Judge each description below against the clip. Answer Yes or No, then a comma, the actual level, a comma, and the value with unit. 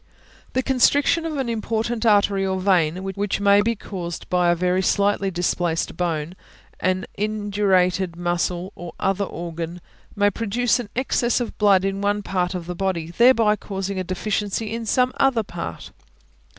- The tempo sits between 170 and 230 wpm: No, average, 160 wpm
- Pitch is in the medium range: No, high, 195 Hz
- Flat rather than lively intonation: No, average, 3.3 semitones